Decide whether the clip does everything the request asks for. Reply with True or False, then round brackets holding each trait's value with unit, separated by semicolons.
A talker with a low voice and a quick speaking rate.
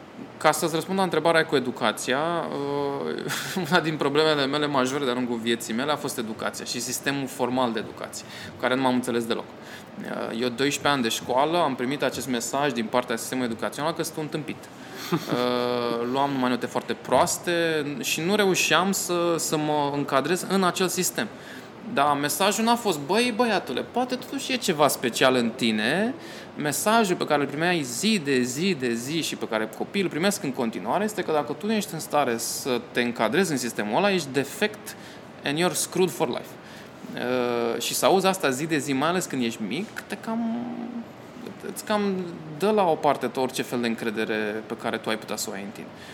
False (145 Hz; 190 wpm)